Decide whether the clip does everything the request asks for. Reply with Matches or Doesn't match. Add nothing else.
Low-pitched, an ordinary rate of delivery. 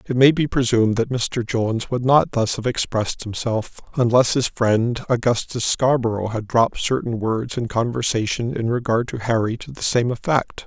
Matches